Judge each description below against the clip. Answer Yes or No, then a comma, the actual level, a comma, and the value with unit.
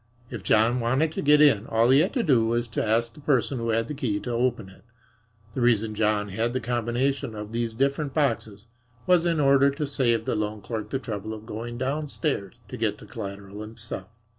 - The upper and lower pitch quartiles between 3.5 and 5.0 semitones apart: Yes, average, 4.1 semitones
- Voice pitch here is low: Yes, low, 120 Hz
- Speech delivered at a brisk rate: Yes, fast, 215 wpm